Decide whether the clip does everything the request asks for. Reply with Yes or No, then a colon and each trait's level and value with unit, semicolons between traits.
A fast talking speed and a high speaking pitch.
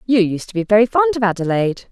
Yes: fast, 250 wpm; high, 215 Hz